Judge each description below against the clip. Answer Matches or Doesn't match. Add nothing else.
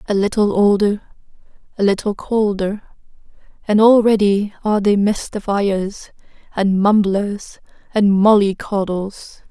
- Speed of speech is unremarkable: Doesn't match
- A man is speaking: Doesn't match